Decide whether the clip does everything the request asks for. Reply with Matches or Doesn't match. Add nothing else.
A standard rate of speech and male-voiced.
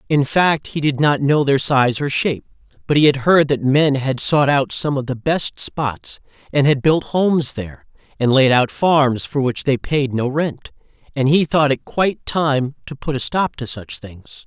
Doesn't match